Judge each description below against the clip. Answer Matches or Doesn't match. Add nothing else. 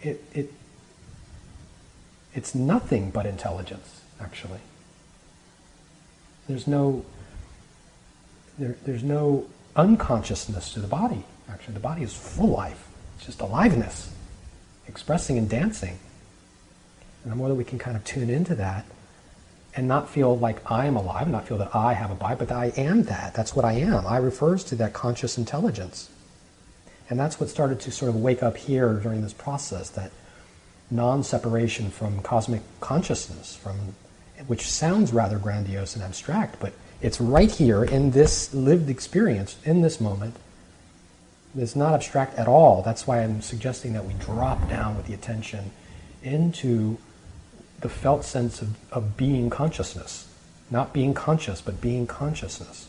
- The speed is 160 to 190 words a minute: Doesn't match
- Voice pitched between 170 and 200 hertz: Doesn't match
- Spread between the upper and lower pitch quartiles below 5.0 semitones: Doesn't match